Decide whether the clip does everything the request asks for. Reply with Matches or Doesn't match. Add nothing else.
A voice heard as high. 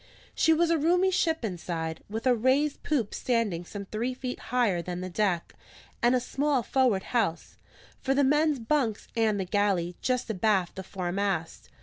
Matches